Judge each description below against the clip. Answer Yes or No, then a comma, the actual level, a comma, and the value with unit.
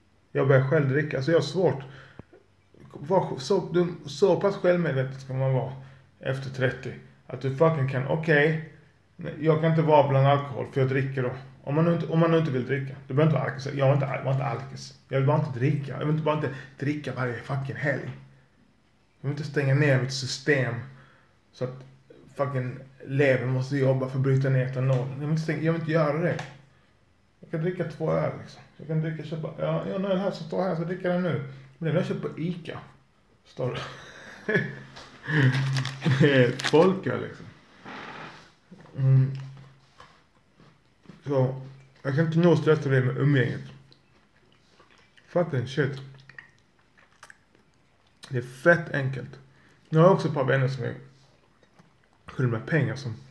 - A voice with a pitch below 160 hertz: Yes, low, 135 Hz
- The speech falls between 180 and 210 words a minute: No, average, 170 wpm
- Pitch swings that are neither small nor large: Yes, average, 3.2 semitones